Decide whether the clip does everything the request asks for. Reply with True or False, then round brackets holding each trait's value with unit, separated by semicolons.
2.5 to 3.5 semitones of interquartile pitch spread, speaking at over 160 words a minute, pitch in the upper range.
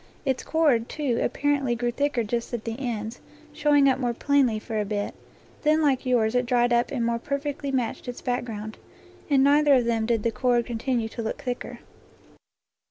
True (3.2 semitones; 190 wpm; 245 Hz)